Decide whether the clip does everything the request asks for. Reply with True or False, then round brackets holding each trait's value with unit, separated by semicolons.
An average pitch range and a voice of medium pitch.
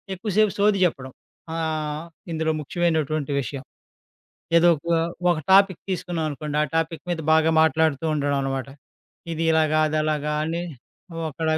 False (2.0 semitones; 160 Hz)